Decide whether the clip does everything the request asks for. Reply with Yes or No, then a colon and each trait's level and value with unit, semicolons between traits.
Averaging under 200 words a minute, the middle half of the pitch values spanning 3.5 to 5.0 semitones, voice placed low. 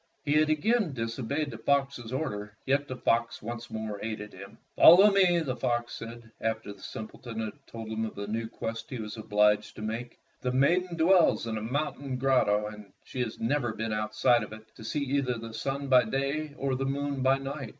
No: fast, 205 wpm; average, 4.1 semitones; low, 120 Hz